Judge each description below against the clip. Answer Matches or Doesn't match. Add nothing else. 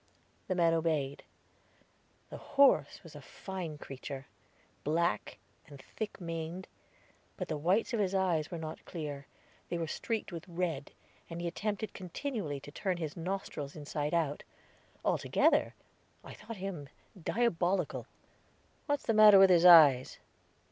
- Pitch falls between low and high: Matches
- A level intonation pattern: Doesn't match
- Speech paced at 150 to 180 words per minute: Doesn't match